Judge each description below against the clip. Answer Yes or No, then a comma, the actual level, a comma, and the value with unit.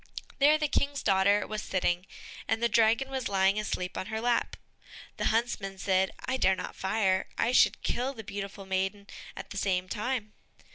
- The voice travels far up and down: No, average, 3.6 semitones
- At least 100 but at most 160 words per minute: No, average, 180 wpm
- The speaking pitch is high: Yes, high, 210 Hz